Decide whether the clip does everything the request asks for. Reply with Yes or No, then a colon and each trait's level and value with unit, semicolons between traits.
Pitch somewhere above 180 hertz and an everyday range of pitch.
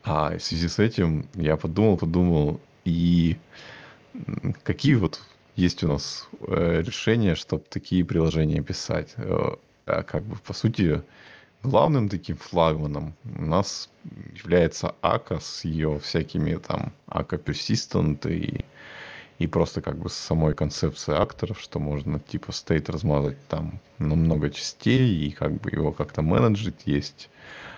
No: very low, 80 Hz; average, 3.2 semitones